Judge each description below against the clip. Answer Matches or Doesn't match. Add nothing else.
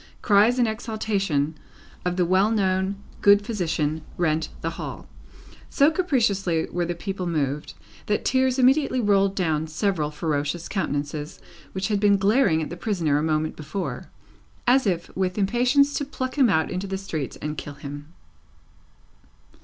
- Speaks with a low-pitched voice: Doesn't match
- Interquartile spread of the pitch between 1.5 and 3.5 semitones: Doesn't match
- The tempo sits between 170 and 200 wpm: Doesn't match